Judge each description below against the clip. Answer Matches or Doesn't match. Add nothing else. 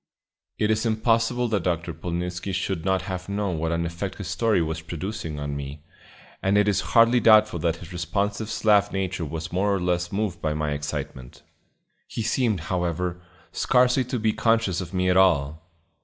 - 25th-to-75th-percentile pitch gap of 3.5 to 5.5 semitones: Matches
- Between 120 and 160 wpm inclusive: Doesn't match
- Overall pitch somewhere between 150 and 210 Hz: Doesn't match